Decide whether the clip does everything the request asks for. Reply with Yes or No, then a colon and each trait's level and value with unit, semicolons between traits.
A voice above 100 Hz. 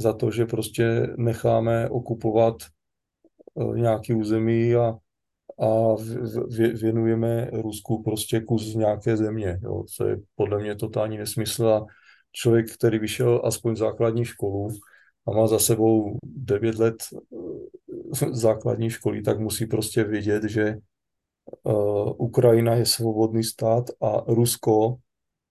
Yes: low, 115 Hz